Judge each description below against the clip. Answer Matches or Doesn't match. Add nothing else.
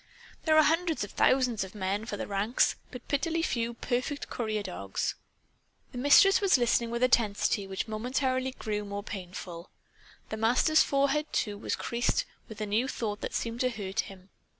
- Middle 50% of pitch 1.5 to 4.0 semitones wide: Doesn't match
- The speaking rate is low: Doesn't match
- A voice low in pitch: Doesn't match